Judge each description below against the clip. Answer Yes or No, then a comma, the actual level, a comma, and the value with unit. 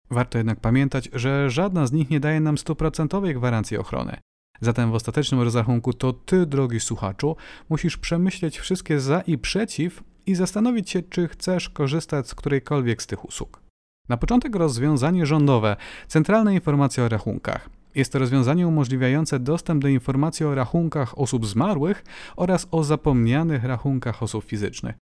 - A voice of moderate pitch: Yes, medium, 145 Hz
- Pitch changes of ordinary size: Yes, average, 4.9 semitones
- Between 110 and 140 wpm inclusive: No, average, 150 wpm